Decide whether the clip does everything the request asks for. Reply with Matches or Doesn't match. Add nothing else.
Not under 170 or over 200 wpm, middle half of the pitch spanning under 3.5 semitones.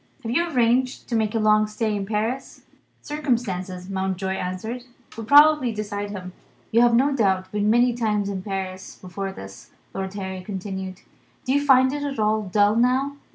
Doesn't match